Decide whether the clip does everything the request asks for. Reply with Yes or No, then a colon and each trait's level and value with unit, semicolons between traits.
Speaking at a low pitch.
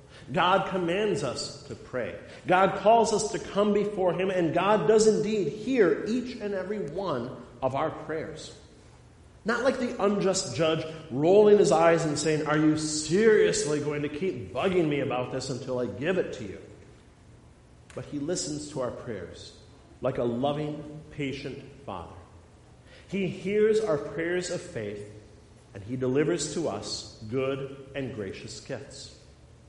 No: medium, 150 Hz